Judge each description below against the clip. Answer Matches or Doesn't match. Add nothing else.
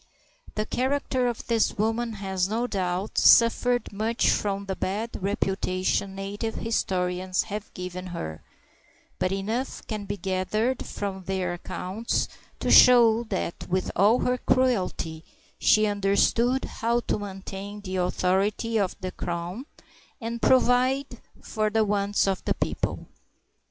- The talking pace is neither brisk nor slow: Doesn't match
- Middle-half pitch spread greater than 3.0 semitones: Matches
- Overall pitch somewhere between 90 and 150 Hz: Doesn't match